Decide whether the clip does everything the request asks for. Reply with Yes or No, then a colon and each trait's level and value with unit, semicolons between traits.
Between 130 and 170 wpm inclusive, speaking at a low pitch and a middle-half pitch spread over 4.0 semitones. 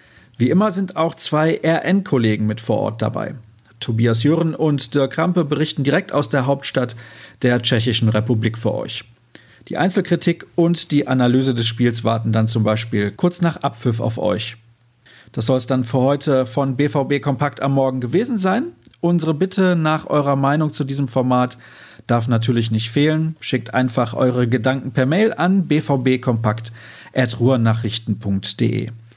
Yes: average, 150 wpm; low, 130 Hz; average, 4.6 semitones